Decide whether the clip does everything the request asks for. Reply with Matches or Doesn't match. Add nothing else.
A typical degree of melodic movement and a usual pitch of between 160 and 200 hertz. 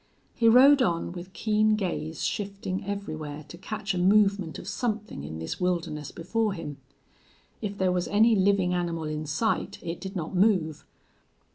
Matches